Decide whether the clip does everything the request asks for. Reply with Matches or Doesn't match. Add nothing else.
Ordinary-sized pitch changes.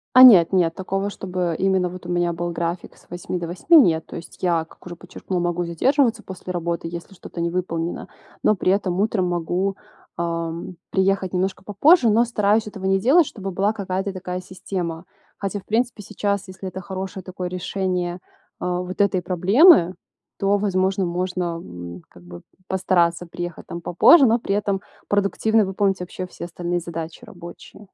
Doesn't match